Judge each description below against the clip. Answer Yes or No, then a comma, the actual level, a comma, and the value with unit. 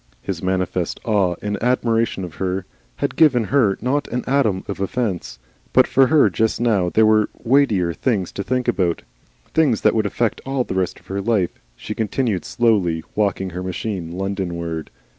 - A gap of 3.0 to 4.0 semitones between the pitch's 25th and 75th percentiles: No, average, 4.4 semitones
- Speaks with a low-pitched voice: Yes, low, 105 Hz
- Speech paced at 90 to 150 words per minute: No, average, 175 wpm